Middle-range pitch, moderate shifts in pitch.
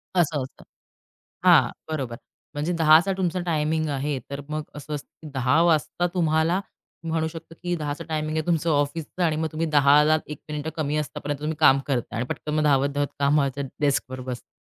No: medium, 150 Hz; narrow, 2.1 semitones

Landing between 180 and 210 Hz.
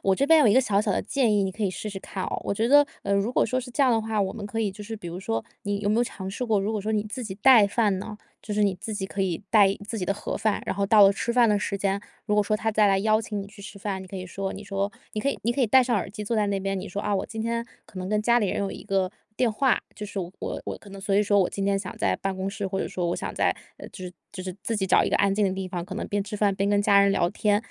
Yes: high, 205 Hz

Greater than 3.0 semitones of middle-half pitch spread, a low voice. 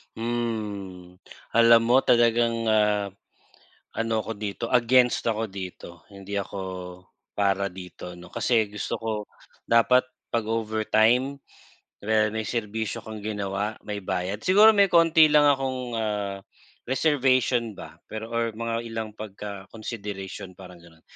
No: average, 2.7 semitones; low, 110 Hz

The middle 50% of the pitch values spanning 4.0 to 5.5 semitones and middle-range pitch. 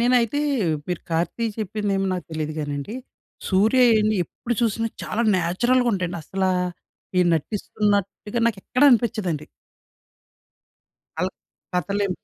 No: average, 4.3 semitones; high, 205 Hz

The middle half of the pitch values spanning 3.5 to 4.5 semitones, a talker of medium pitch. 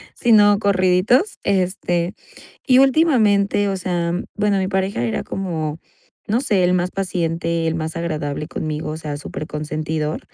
Yes: average, 4.0 semitones; medium, 180 Hz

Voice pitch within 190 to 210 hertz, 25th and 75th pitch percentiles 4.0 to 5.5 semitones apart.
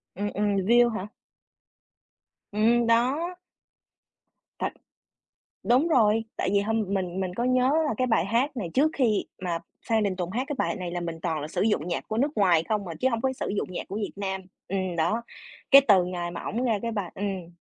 Yes: high, 205 Hz; average, 4.4 semitones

